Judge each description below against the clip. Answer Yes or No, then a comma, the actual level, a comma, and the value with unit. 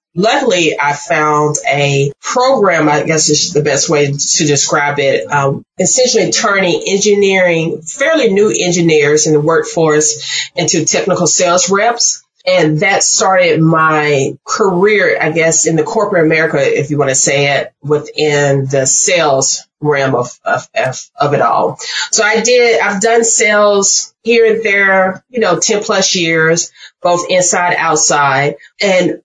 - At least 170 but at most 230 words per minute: No, average, 150 wpm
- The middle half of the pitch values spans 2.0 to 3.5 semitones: No, average, 5.3 semitones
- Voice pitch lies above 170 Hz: No, medium, 160 Hz